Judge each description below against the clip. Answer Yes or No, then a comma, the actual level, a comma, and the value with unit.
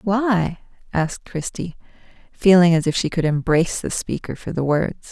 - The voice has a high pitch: No, medium, 175 Hz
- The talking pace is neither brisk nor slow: Yes, average, 165 wpm